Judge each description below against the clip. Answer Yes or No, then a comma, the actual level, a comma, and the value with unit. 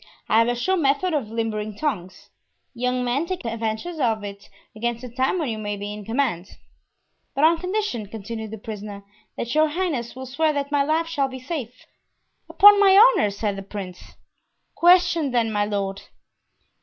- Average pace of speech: Yes, average, 180 wpm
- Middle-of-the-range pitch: No, high, 245 Hz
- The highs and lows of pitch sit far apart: Yes, wide, 6.5 semitones